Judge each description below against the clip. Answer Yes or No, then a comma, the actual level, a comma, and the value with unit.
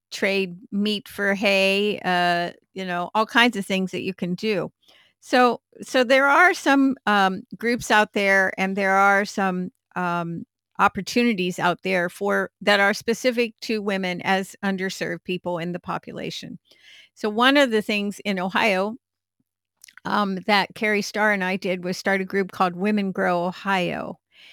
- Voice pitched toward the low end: No, high, 195 Hz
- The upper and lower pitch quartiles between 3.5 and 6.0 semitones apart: No, narrow, 2.4 semitones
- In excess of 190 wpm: No, average, 160 wpm